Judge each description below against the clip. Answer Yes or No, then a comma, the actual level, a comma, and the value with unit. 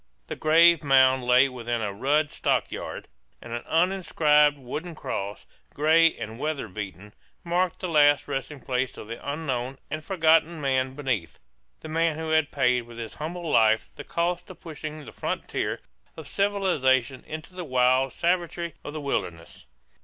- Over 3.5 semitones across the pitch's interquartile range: Yes, average, 4.5 semitones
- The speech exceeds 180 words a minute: No, average, 160 wpm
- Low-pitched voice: No, medium, 145 Hz